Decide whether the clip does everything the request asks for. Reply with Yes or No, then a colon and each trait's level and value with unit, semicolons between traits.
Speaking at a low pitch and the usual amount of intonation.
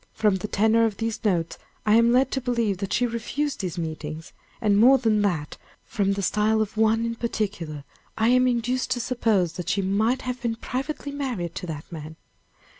No: high, 220 Hz; average, 4.0 semitones